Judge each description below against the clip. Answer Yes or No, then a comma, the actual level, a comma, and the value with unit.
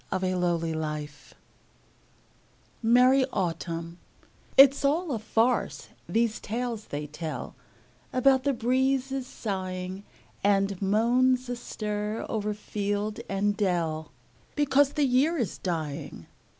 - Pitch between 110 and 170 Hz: No, high, 210 Hz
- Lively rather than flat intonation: Yes, wide, 5.7 semitones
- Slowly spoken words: Yes, slow, 105 wpm